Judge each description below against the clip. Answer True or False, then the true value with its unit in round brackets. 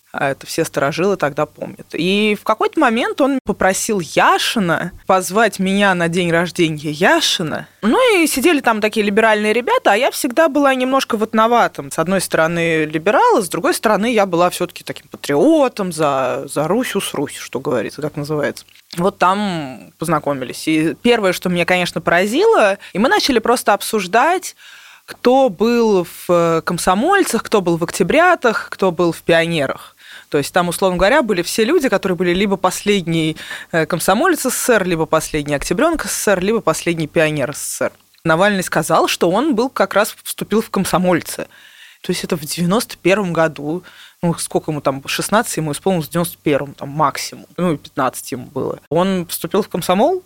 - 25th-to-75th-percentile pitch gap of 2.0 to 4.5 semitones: False (5.4 semitones)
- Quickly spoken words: True (165 wpm)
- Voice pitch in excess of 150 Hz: True (185 Hz)